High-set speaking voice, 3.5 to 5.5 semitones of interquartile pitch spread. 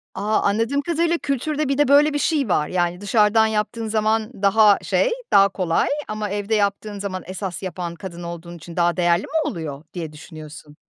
Yes: high, 205 Hz; average, 4.4 semitones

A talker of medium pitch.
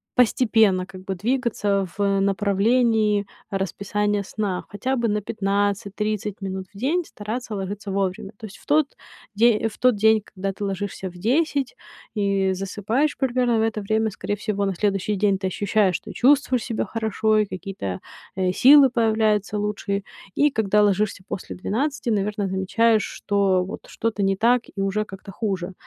No: high, 205 Hz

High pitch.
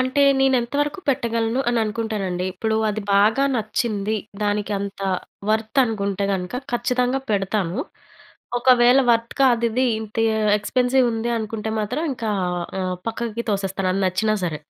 Yes: high, 220 Hz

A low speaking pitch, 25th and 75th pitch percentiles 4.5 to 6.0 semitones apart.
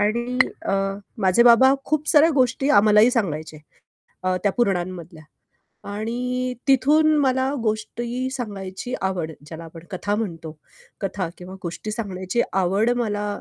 No: high, 210 Hz; average, 5.1 semitones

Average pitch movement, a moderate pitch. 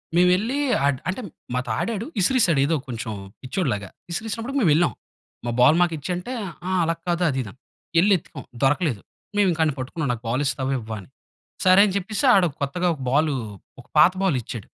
No: wide, 6.2 semitones; medium, 165 Hz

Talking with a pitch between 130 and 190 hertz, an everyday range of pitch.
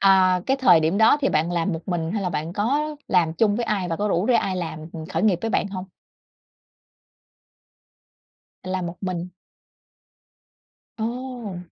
Yes: medium, 185 Hz; average, 4.3 semitones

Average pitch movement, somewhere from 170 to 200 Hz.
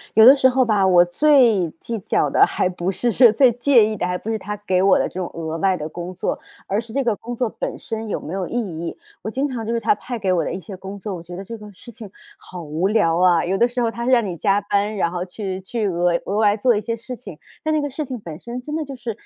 No: average, 4.5 semitones; high, 210 Hz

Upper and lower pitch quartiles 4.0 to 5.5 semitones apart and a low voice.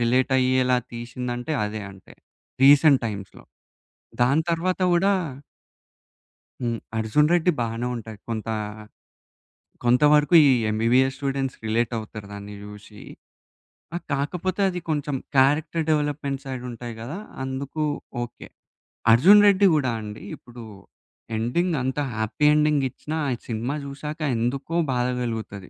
Yes: average, 4.5 semitones; low, 130 Hz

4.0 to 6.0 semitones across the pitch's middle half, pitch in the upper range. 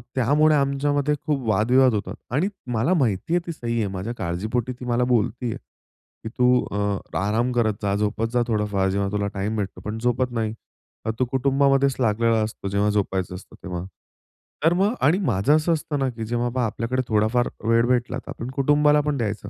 No: average, 4.5 semitones; low, 120 Hz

